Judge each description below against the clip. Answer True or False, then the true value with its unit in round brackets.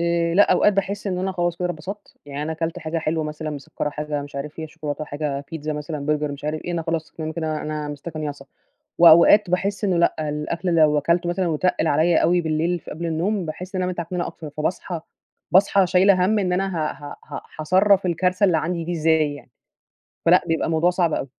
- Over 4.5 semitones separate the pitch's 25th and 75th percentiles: False (2.9 semitones)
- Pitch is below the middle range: False (165 Hz)